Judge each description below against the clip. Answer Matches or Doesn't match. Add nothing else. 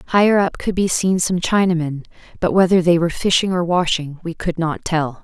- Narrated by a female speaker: Matches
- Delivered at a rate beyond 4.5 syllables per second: Matches